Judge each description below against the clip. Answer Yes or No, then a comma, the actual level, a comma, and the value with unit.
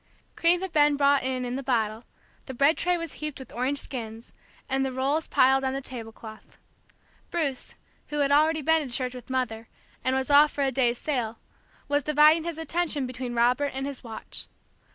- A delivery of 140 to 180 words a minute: No, average, 195 wpm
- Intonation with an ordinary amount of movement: Yes, average, 3.0 semitones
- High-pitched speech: Yes, very high, 270 Hz